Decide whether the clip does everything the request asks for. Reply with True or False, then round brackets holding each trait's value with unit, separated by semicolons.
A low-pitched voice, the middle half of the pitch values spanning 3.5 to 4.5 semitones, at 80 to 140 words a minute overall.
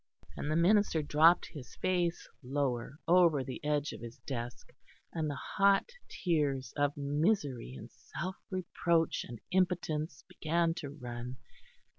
False (150 Hz; 4.2 semitones; 135 wpm)